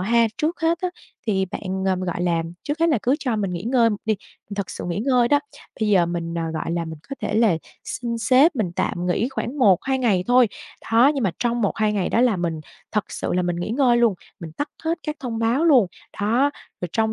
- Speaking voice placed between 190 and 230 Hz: Yes, high, 225 Hz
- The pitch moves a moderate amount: No, wide, 5.8 semitones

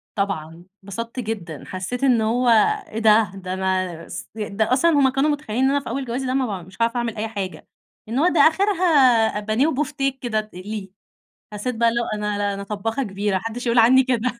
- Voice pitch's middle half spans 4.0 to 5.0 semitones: Yes, average, 4.3 semitones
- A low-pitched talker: No, high, 225 Hz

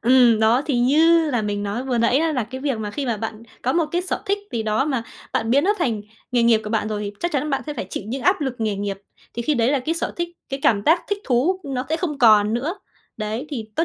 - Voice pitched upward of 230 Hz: Yes, very high, 250 Hz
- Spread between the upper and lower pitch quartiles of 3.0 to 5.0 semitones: No, wide, 5.4 semitones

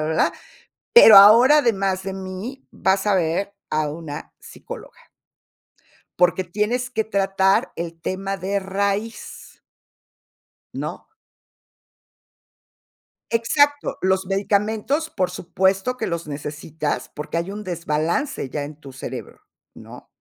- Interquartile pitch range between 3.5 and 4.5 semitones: Yes, average, 4.0 semitones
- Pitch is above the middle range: Yes, high, 195 Hz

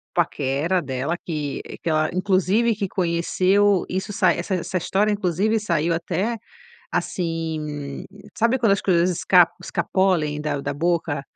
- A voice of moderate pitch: Yes, medium, 175 Hz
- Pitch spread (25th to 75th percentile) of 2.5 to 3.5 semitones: No, average, 3.9 semitones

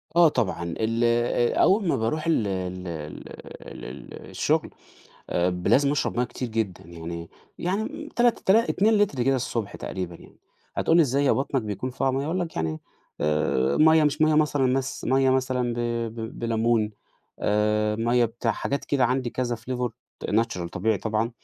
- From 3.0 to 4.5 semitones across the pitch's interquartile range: No, average, 4.9 semitones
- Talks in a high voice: No, low, 120 Hz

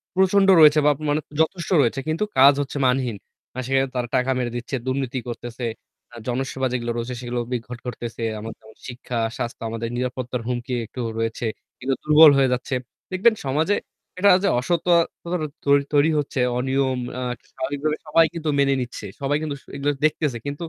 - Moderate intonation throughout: Yes, average, 3.6 semitones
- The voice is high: No, low, 135 Hz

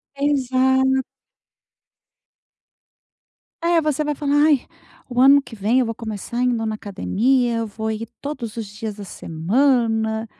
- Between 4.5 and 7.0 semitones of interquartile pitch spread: No, average, 3.4 semitones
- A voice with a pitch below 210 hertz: No, high, 240 Hz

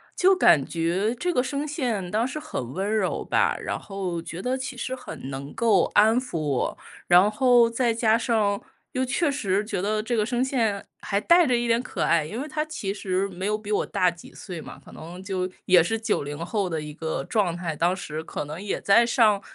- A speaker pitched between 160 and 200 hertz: No, high, 210 Hz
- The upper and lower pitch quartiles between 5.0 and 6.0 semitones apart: Yes, average, 5.3 semitones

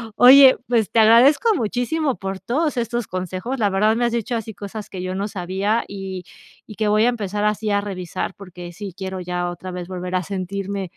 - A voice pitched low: No, high, 200 Hz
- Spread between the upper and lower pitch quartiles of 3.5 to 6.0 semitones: Yes, average, 3.8 semitones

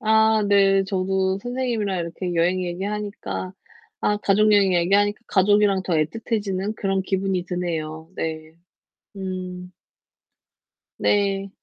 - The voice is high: Yes, high, 195 Hz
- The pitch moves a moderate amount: No, narrow, 2.3 semitones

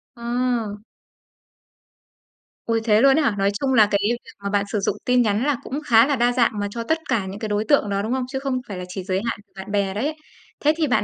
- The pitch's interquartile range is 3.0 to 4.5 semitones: Yes, average, 3.9 semitones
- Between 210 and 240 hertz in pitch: Yes, high, 225 Hz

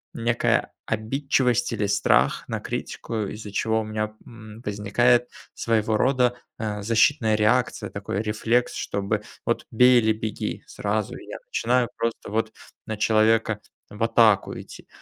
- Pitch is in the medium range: No, low, 110 Hz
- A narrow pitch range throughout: Yes, narrow, 2.1 semitones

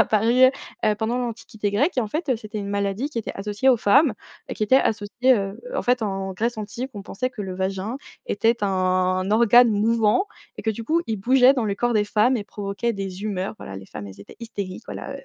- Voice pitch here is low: No, high, 215 Hz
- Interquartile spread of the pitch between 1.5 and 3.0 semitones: No, average, 3.4 semitones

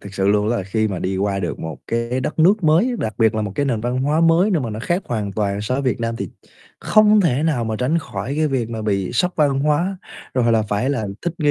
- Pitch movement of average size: No, wide, 6.4 semitones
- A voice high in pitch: No, low, 120 Hz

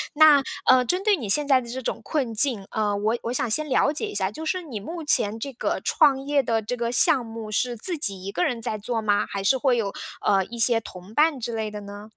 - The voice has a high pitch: Yes, high, 235 Hz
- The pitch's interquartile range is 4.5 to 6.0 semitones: Yes, average, 5.1 semitones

